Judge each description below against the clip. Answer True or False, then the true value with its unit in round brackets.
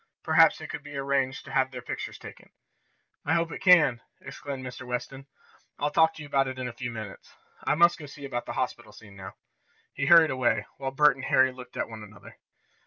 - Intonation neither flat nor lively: True (3.3 semitones)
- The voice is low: True (130 Hz)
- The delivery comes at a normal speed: False (220 wpm)